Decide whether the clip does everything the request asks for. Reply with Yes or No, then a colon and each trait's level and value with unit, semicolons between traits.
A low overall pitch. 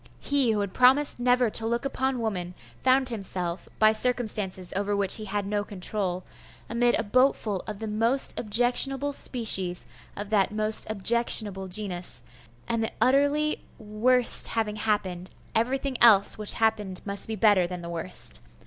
No: high, 215 Hz